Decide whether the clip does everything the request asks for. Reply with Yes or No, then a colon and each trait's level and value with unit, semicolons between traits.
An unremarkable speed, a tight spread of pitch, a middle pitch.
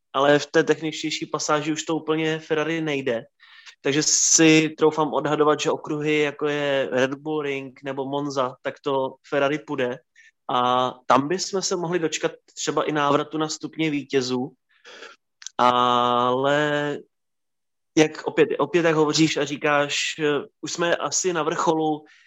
Yes: average, 140 wpm; narrow, 2.3 semitones; medium, 150 Hz